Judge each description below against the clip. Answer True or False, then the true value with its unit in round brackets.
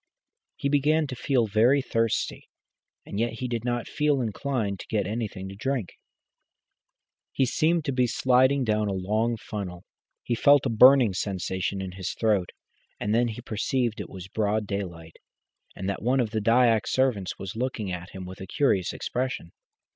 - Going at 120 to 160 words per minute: False (175 wpm)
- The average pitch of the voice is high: False (115 Hz)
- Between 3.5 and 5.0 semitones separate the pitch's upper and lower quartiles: True (4.5 semitones)